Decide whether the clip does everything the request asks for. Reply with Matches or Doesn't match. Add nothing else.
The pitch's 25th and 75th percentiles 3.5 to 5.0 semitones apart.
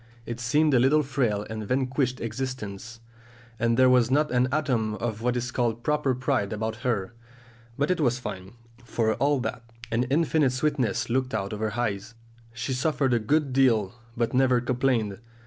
Doesn't match